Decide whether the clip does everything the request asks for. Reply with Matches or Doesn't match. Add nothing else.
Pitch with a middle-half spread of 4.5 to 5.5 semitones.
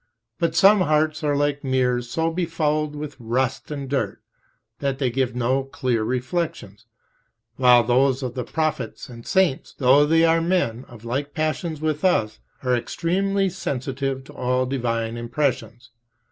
Doesn't match